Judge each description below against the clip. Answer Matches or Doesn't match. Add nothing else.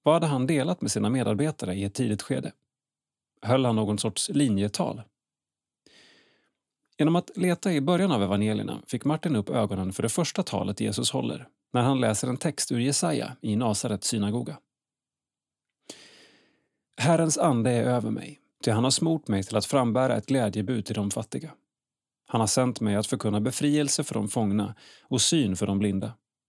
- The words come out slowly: Doesn't match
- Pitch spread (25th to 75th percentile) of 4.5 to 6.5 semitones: Matches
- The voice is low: Matches